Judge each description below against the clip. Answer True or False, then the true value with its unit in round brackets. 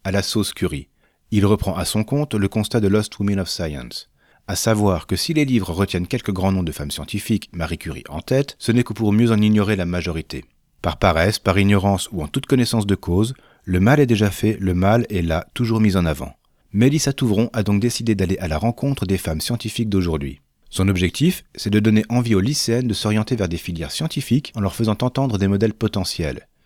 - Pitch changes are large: False (4.2 semitones)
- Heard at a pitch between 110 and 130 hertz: False (100 Hz)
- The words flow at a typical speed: False (225 wpm)